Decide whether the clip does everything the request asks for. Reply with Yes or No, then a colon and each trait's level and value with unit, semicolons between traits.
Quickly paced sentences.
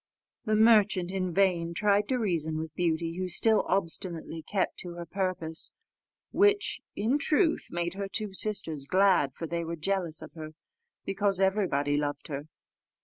No: average, 155 wpm